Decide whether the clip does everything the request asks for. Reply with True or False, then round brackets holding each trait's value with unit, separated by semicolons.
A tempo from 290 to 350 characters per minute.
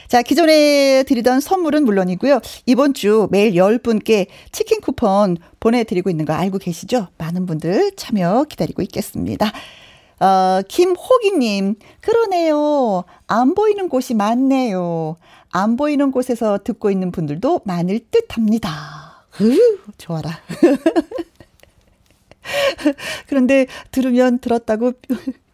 False (250 characters per minute)